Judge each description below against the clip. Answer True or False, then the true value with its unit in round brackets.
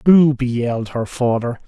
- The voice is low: True (125 Hz)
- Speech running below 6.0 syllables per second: True (4.6 syllables/s)